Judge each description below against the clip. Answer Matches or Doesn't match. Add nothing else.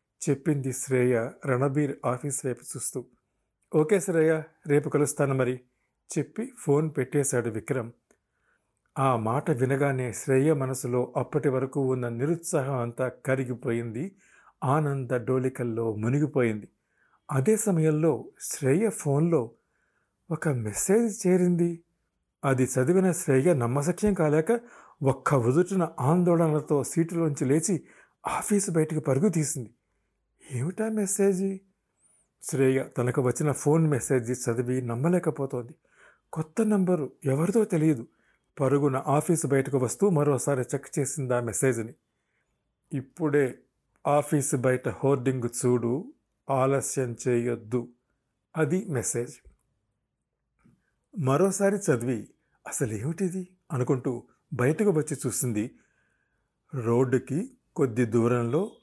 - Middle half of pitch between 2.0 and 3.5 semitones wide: Doesn't match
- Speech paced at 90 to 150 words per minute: Matches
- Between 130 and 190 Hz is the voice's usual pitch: Matches